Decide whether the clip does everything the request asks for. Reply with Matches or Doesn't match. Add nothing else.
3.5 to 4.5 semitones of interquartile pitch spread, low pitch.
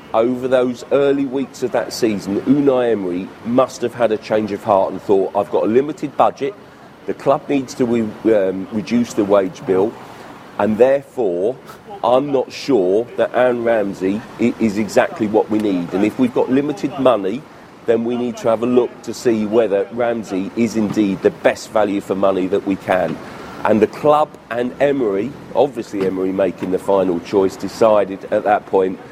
Matches